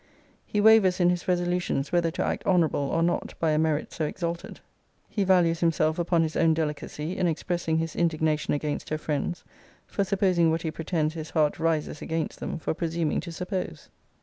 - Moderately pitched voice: Yes, medium, 165 Hz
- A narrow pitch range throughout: Yes, narrow, 2.1 semitones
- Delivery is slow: No, average, 185 wpm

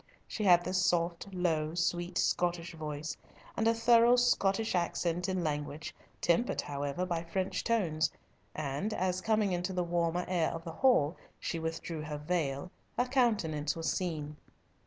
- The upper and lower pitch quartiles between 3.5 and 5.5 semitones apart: No, average, 3.1 semitones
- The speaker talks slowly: No, average, 155 wpm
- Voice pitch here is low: No, medium, 175 Hz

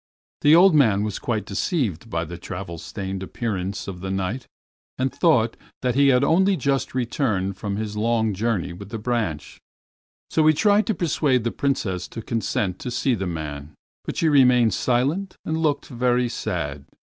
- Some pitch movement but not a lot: No, wide, 6.2 semitones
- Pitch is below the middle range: Yes, low, 115 Hz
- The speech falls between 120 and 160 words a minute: No, average, 175 wpm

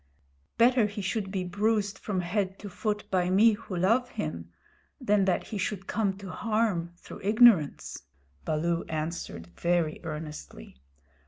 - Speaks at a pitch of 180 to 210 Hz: Yes, high, 190 Hz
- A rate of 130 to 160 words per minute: Yes, average, 145 wpm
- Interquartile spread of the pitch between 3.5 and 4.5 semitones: Yes, average, 3.8 semitones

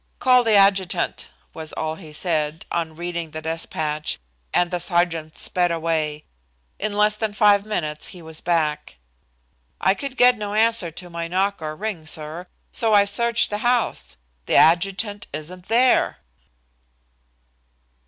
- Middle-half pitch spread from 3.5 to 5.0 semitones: Yes, average, 4.6 semitones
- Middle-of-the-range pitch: Yes, medium, 175 Hz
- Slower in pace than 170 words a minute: Yes, average, 145 wpm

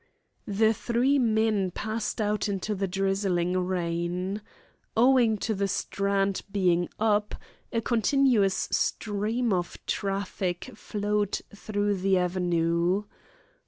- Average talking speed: No, slow, 105 wpm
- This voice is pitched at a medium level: No, high, 200 Hz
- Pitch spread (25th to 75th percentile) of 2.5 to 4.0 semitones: Yes, average, 2.8 semitones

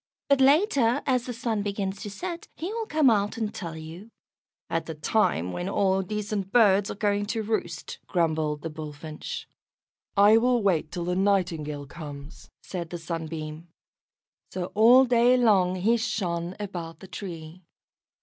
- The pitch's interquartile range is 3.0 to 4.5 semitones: No, wide, 5.4 semitones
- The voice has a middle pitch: No, high, 195 Hz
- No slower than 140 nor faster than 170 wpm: Yes, average, 160 wpm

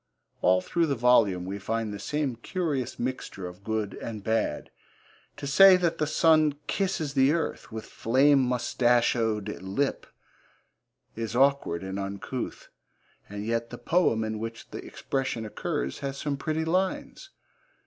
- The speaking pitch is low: Yes, low, 120 Hz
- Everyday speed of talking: Yes, average, 145 wpm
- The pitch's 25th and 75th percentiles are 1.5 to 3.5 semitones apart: No, average, 5.1 semitones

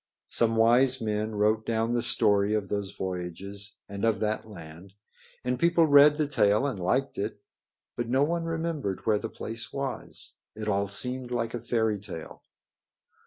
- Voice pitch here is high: No, low, 110 Hz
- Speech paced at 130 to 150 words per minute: No, average, 165 wpm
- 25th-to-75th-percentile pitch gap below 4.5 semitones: Yes, average, 3.9 semitones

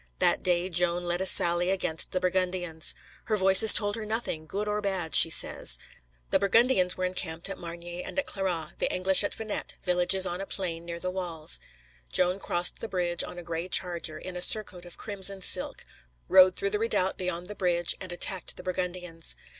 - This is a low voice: No, medium, 180 Hz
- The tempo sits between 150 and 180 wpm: No, average, 195 wpm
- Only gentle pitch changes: Yes, narrow, 1.8 semitones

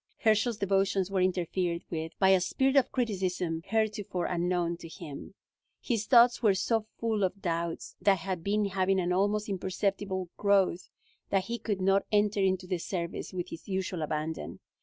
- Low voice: No, high, 190 Hz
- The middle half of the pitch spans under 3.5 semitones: Yes, narrow, 2.6 semitones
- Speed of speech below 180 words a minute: Yes, average, 165 wpm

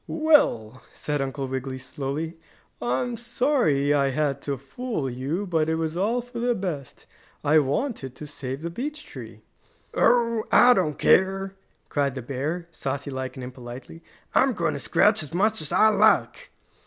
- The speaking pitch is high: No, medium, 155 Hz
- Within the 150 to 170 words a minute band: Yes, average, 165 wpm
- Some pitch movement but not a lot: No, wide, 8.2 semitones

